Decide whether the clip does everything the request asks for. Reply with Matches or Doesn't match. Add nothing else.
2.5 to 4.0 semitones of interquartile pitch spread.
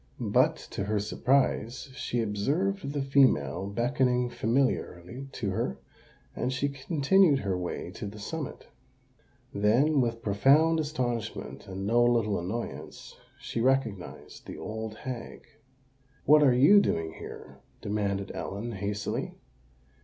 Doesn't match